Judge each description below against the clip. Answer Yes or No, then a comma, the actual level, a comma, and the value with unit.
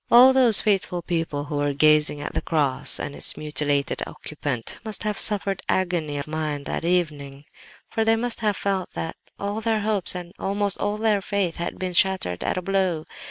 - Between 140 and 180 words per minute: No, average, 190 wpm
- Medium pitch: Yes, medium, 180 Hz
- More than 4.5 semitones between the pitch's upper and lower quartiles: Yes, average, 5.3 semitones